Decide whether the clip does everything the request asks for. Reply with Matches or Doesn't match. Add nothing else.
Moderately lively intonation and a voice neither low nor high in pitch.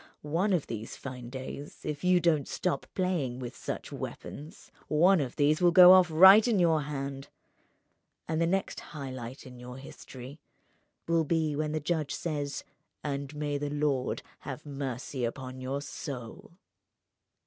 Matches